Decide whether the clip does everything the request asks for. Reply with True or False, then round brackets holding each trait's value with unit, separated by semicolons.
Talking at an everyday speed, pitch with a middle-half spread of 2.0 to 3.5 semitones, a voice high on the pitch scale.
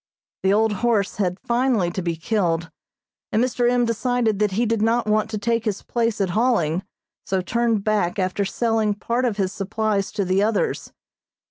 True (180 wpm; 3.1 semitones; 215 Hz)